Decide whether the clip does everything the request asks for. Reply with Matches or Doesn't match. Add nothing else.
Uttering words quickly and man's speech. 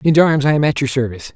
Matches